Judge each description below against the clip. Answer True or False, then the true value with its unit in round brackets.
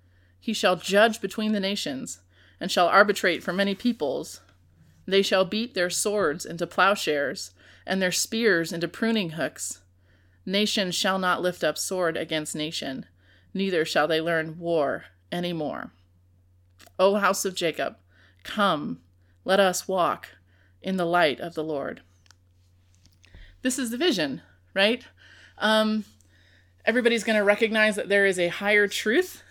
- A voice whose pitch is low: False (170 Hz)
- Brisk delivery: False (140 wpm)